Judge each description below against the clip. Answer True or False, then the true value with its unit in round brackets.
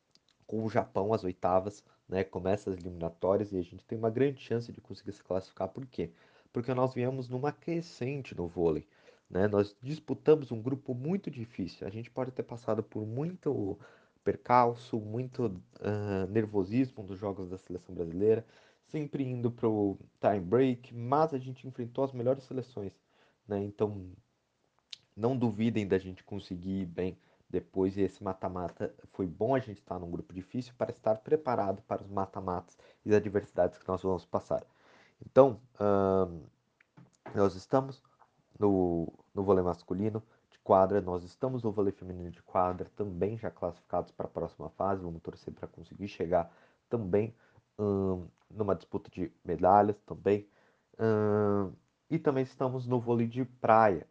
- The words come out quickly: False (160 wpm)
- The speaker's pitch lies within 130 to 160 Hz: False (105 Hz)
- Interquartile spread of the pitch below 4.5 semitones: False (4.8 semitones)